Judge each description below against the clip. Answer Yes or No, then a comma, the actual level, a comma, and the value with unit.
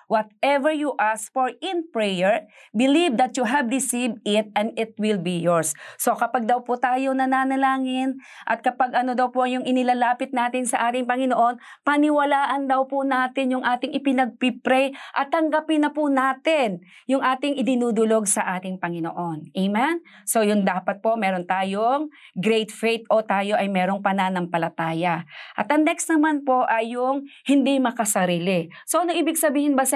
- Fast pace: Yes, fast, 160 wpm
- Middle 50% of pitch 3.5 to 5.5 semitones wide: Yes, average, 4.3 semitones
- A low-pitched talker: No, very high, 250 Hz